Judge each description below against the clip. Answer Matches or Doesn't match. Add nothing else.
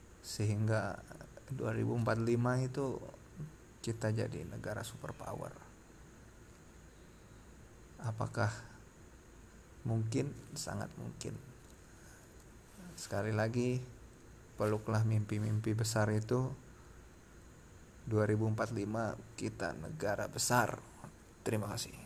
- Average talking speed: Doesn't match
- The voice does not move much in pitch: Matches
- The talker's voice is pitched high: Doesn't match